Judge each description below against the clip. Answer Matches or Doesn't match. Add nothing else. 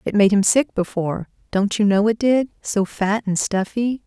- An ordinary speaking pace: Matches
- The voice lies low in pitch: Doesn't match